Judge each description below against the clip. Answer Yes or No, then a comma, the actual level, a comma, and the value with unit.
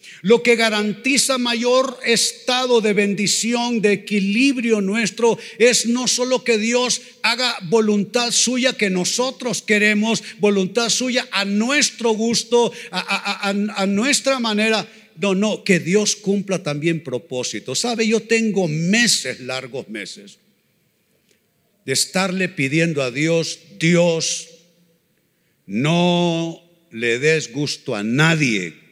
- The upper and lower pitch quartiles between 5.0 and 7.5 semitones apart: Yes, wide, 5.5 semitones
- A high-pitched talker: Yes, high, 205 Hz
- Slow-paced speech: Yes, slow, 120 wpm